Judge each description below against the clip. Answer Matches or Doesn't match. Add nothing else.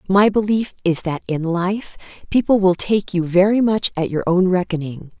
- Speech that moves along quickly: Doesn't match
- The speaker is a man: Doesn't match